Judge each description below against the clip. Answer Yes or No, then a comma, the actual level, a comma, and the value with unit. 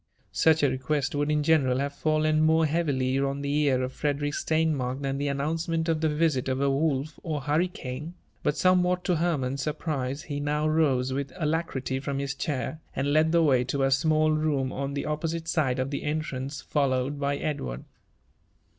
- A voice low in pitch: No, medium, 145 Hz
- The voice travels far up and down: No, narrow, 2.6 semitones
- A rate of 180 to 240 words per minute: Yes, average, 190 wpm